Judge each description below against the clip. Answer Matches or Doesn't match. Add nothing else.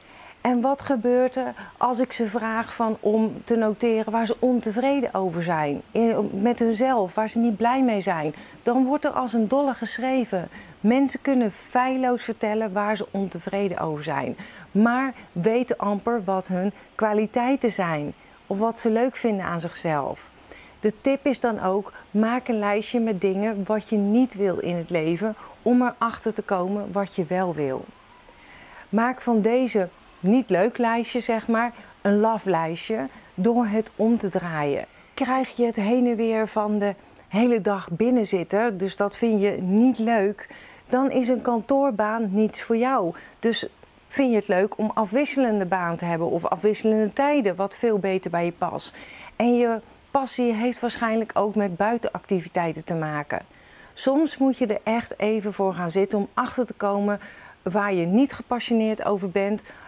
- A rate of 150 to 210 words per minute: Matches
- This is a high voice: Matches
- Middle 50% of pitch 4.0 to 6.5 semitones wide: Doesn't match